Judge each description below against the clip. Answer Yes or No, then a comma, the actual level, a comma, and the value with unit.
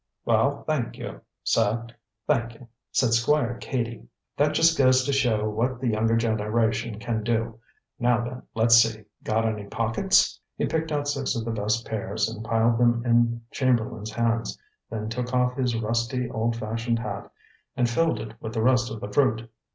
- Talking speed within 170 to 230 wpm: Yes, average, 175 wpm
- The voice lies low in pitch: Yes, low, 115 Hz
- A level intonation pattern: Yes, narrow, 1.9 semitones